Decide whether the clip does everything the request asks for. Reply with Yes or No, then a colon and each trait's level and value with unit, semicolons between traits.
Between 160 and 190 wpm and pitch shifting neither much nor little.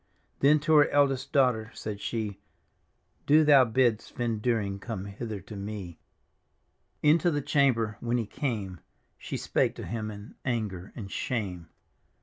No: average, 150 wpm; average, 4.6 semitones